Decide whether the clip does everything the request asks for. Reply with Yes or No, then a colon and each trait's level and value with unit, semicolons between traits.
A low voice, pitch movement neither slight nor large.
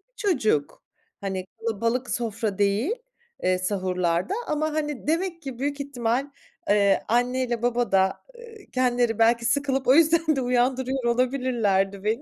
No: high, 245 Hz; average, 4.8 semitones